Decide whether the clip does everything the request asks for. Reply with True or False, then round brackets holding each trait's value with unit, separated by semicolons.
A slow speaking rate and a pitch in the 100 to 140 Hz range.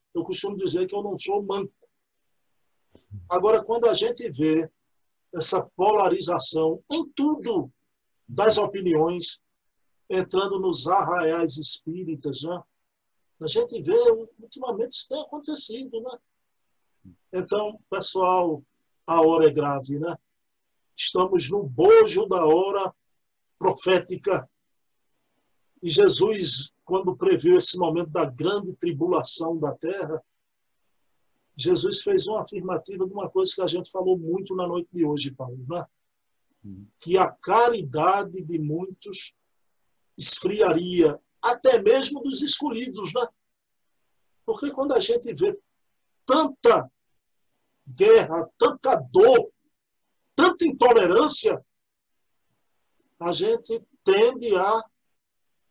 False (110 wpm; 195 Hz)